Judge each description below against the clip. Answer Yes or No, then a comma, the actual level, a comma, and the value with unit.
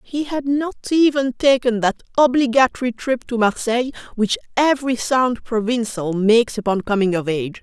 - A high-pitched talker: Yes, high, 240 Hz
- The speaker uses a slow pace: No, average, 150 wpm